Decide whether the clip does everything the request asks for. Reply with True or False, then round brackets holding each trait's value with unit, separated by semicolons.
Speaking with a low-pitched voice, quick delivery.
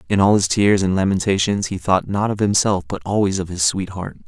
True (95 Hz; 225 wpm)